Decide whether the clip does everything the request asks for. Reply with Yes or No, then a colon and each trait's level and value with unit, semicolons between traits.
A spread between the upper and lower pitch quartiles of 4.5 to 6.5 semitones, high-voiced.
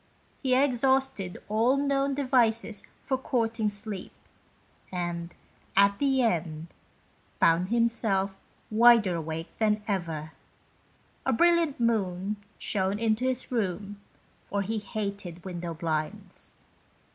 Yes: average, 5.0 semitones; high, 210 Hz